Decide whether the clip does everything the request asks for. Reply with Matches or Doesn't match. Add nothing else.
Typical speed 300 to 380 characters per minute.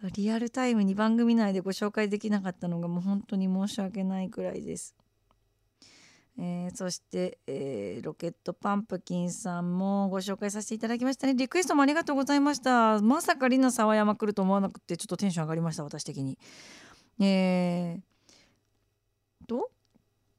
Matches